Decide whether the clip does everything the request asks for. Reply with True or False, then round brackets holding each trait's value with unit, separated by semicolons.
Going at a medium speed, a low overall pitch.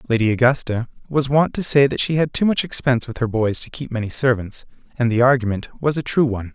False (240 wpm; 130 Hz)